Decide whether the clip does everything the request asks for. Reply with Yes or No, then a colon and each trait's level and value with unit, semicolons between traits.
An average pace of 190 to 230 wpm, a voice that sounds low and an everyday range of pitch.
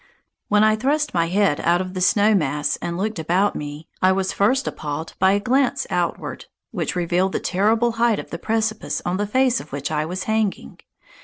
No: fast, 205 wpm; high, 190 Hz; average, 4.4 semitones